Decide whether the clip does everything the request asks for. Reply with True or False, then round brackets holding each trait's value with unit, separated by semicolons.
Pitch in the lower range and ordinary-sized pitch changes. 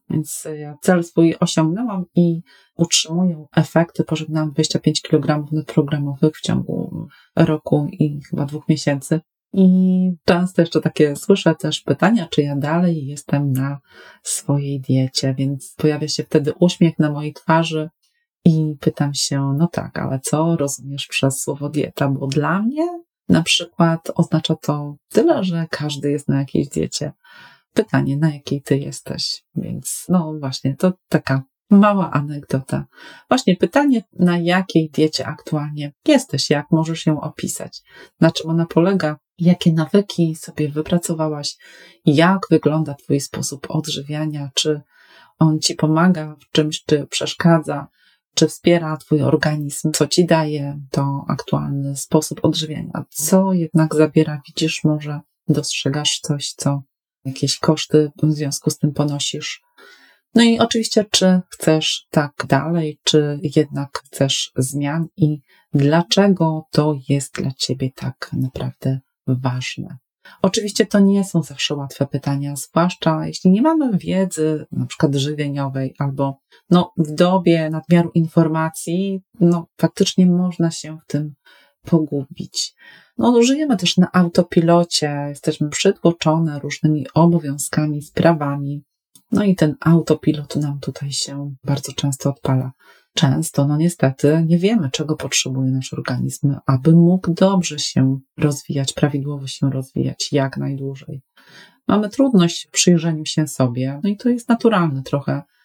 False (155 Hz; 3.2 semitones)